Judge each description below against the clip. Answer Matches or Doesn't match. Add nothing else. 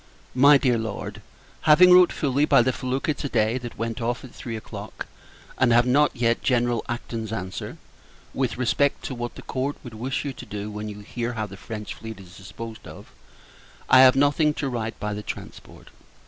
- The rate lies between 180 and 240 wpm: Matches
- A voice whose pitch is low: Matches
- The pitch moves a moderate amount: Matches